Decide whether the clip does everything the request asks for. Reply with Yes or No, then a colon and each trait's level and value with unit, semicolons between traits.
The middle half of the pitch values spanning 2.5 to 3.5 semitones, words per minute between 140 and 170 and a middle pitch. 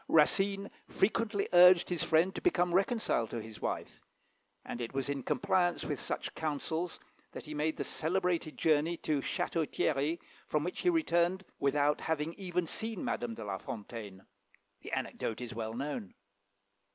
No: average, 4.7 semitones; average, 160 wpm; medium, 160 Hz